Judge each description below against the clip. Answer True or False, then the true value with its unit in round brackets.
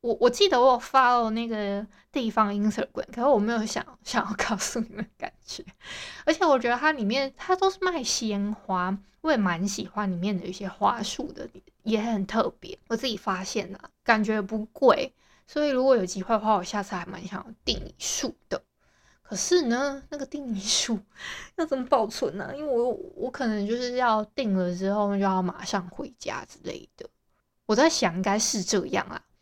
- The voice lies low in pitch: False (225 Hz)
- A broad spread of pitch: False (4.7 semitones)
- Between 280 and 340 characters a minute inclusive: True (290 characters per minute)